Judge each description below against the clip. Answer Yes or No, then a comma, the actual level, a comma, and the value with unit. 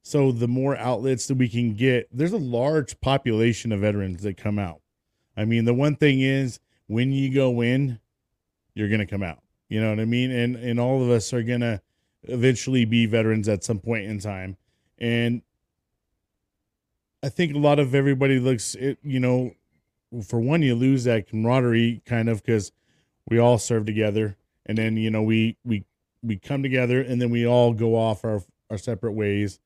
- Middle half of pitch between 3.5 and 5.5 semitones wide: No, average, 2.9 semitones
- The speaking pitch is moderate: No, low, 120 Hz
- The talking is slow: No, average, 195 wpm